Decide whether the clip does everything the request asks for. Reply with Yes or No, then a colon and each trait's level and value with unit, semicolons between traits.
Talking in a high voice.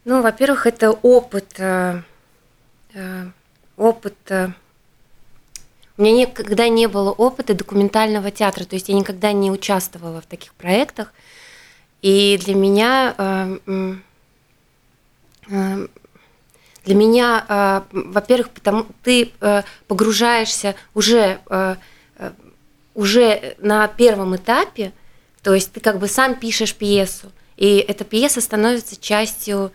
Yes: high, 200 Hz